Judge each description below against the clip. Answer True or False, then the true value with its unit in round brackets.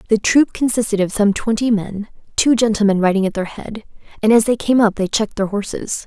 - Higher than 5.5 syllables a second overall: True (5.8 syllables/s)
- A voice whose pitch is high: True (215 Hz)